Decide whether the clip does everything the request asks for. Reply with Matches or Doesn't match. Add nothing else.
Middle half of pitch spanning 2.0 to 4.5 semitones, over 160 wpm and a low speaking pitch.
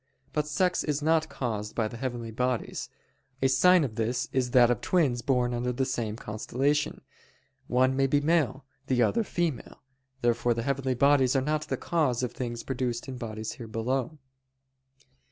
Matches